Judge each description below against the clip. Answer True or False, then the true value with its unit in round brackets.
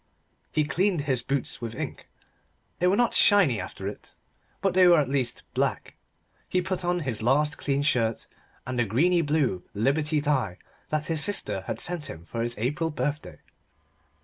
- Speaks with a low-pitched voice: False (145 Hz)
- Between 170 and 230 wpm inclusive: True (175 wpm)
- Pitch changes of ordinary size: False (6.1 semitones)